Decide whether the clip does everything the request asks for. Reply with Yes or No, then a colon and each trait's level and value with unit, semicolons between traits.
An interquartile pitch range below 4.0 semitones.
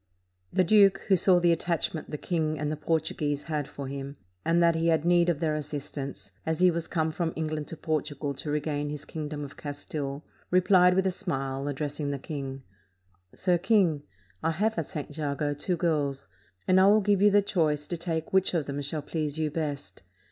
Yes: average, 3.1 semitones